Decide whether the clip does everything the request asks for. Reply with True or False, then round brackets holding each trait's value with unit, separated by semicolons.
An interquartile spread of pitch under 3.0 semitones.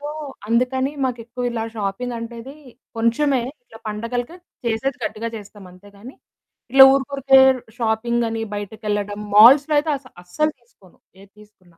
False (3.7 semitones)